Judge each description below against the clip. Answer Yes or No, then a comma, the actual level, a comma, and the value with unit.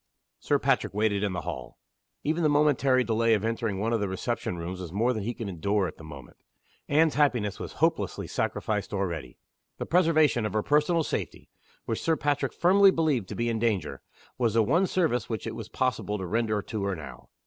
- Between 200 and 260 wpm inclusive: Yes, fast, 205 wpm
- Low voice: Yes, low, 115 Hz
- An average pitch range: No, wide, 6.5 semitones